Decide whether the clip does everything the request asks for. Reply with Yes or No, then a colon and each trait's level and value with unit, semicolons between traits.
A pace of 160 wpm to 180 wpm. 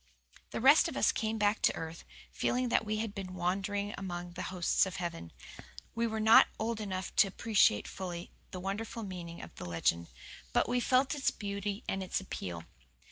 No: average, 190 wpm